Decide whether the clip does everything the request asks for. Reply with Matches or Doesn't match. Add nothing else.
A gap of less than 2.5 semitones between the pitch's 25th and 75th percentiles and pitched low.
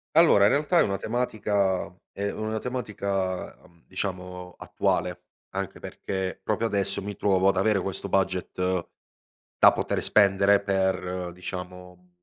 Matches